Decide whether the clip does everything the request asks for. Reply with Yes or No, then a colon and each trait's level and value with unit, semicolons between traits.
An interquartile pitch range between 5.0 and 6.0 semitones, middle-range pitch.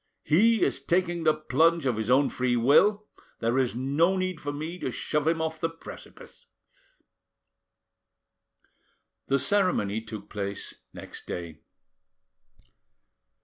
Yes: wide, 5.6 semitones; medium, 145 Hz